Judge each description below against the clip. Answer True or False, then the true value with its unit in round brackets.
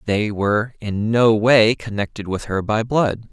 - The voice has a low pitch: True (110 Hz)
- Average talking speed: True (180 wpm)